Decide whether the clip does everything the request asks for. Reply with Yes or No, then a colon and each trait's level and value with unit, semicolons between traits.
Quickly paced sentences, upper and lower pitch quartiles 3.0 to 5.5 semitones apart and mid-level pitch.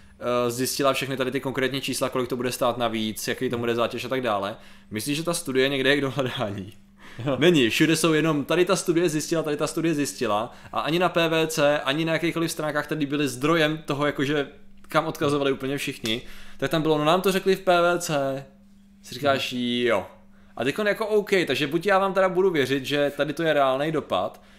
Yes: fast, 205 wpm; average, 3.9 semitones; medium, 145 Hz